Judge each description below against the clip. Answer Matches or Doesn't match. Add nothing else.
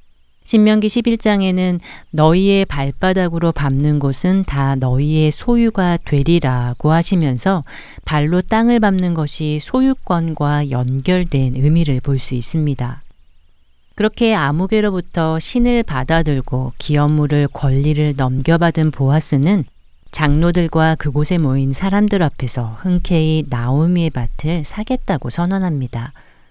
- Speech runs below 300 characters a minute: Matches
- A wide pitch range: Doesn't match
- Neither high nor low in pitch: Matches